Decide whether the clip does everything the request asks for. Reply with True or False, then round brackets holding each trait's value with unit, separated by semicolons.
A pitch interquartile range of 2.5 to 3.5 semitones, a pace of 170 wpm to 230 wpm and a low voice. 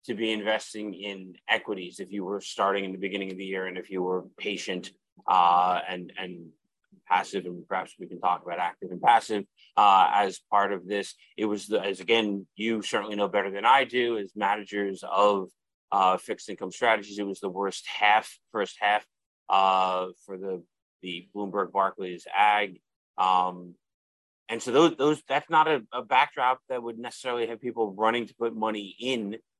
True (3.2 semitones; 185 wpm; 100 Hz)